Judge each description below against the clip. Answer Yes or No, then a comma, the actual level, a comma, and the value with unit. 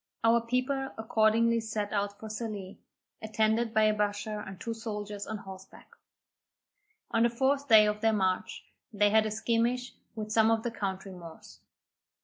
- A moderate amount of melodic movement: No, narrow, 1.8 semitones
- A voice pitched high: Yes, high, 220 Hz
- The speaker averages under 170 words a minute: Yes, average, 160 wpm